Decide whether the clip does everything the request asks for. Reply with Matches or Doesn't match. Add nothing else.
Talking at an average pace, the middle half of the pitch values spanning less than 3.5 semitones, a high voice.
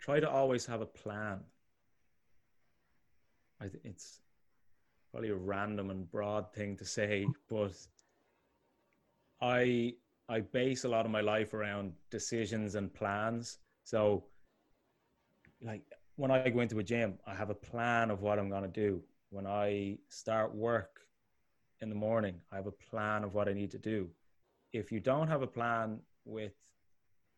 Doesn't match